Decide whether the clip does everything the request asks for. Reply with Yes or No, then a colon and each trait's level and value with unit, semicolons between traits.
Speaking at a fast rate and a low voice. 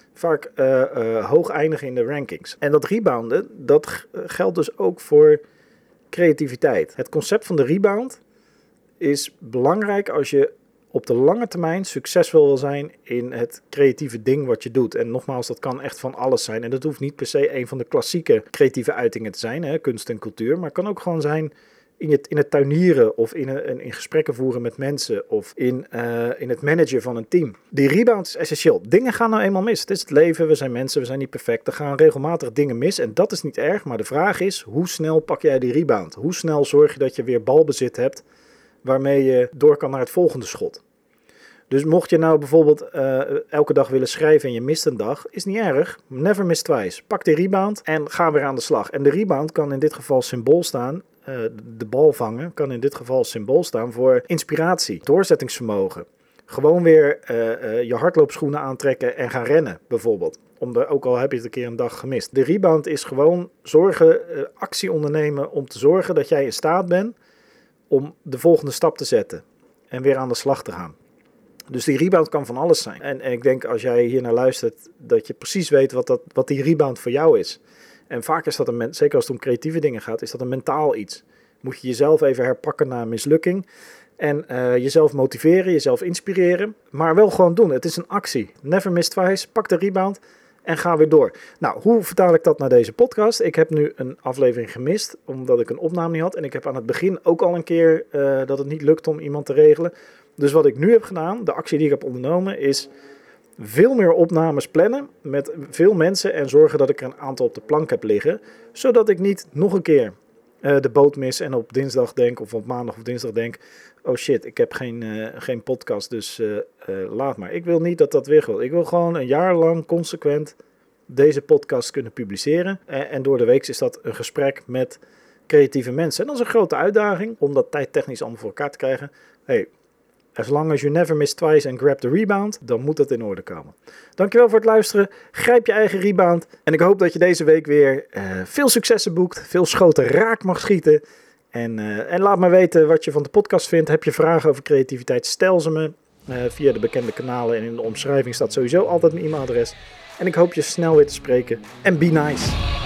No: fast, 225 wpm; medium, 170 Hz